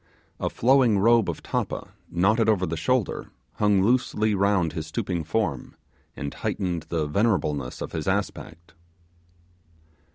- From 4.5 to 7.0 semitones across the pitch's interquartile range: Yes, average, 5.1 semitones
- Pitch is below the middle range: Yes, very low, 95 Hz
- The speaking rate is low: Yes, slow, 130 wpm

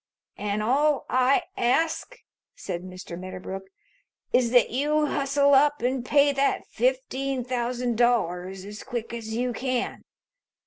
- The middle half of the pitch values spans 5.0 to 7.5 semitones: No, average, 4.3 semitones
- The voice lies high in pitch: Yes, high, 245 Hz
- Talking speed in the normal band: No, slow, 130 wpm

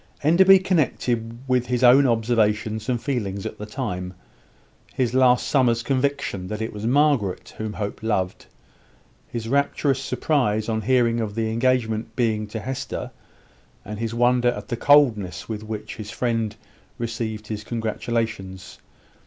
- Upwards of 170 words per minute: No, average, 145 wpm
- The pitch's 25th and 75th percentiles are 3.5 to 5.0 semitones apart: No, average, 2.9 semitones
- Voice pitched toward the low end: Yes, low, 115 Hz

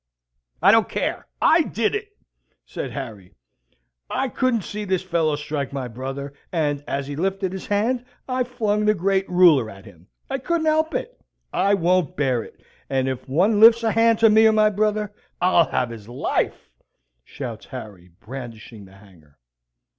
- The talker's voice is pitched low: No, medium, 180 Hz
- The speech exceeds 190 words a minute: No, average, 170 wpm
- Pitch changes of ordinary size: No, wide, 8.9 semitones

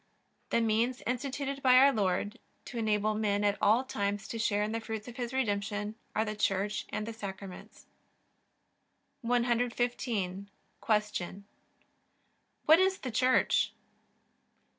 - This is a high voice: Yes, high, 220 Hz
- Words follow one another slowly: Yes, slow, 130 wpm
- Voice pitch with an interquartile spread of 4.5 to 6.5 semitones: No, average, 3.1 semitones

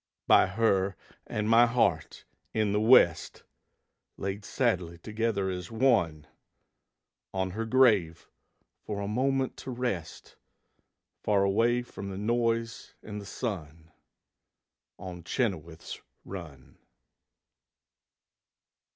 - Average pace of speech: No, slow, 100 wpm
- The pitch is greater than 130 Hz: No, low, 100 Hz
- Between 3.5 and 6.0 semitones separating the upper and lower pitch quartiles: Yes, average, 4.3 semitones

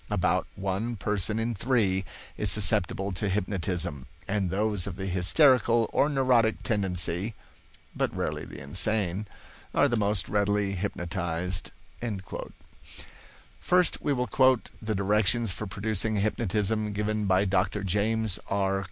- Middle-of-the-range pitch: No, low, 105 Hz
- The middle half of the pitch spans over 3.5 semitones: No, average, 2.7 semitones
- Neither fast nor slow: No, slow, 125 wpm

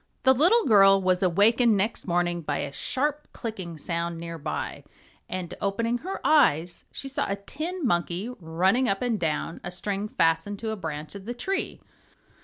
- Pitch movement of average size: No, wide, 5.8 semitones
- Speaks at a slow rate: No, average, 175 wpm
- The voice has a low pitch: No, high, 195 Hz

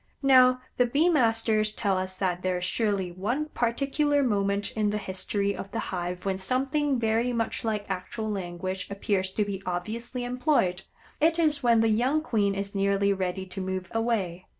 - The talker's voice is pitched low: No, high, 210 Hz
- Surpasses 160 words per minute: Yes, average, 175 wpm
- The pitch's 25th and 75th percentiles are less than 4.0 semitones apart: No, average, 4.4 semitones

